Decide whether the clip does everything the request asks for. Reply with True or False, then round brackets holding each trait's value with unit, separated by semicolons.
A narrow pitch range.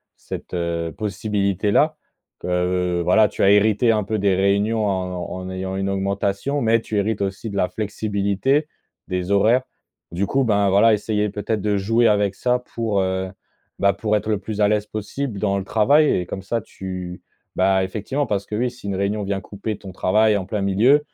True (2.2 semitones)